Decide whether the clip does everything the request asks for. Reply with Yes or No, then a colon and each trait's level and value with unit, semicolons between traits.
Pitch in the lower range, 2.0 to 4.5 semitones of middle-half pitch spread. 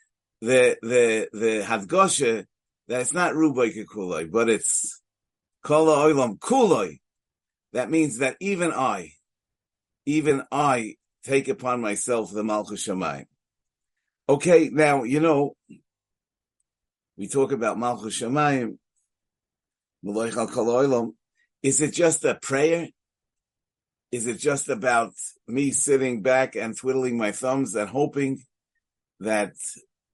No: low, 130 Hz; average, 5.0 semitones